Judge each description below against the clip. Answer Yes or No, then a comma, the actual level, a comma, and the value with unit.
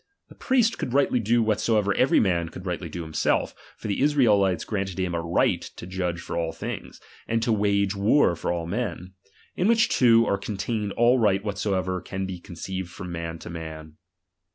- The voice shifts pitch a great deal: No, average, 4.5 semitones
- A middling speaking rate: Yes, average, 190 wpm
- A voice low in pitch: Yes, very low, 95 Hz